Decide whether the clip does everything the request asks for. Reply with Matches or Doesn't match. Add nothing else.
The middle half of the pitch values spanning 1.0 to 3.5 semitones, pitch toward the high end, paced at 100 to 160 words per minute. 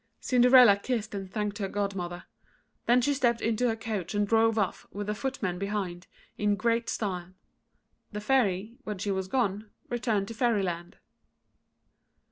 Matches